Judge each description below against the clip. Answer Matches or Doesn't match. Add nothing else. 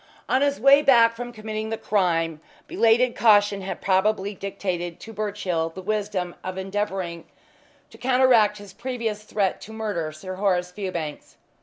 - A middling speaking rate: Matches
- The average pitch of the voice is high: Matches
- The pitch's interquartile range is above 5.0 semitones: Doesn't match